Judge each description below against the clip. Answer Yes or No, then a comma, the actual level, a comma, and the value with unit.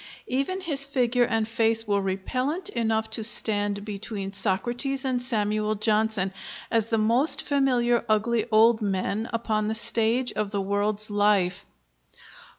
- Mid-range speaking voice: No, high, 220 Hz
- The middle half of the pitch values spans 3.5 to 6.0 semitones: No, average, 2.7 semitones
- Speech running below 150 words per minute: Yes, average, 140 wpm